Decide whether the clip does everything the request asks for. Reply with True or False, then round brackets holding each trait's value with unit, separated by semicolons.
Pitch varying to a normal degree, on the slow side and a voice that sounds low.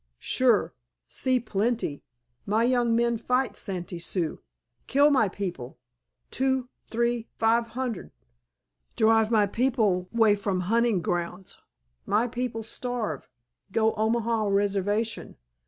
False (3.2 semitones; 110 wpm; 225 Hz)